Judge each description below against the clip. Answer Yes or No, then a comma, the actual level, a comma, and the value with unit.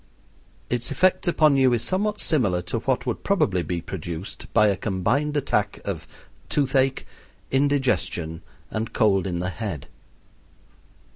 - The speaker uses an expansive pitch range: Yes, wide, 7.1 semitones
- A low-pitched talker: Yes, low, 115 Hz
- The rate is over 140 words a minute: No, slow, 135 wpm